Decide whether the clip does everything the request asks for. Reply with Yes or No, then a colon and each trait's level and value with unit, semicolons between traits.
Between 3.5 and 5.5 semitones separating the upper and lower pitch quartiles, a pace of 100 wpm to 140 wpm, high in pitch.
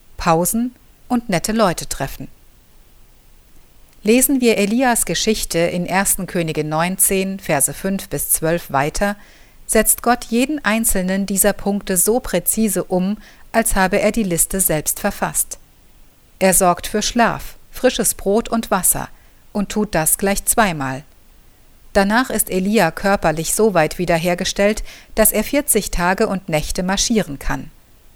Yes: average, 3.9 semitones; average, 130 wpm; high, 200 Hz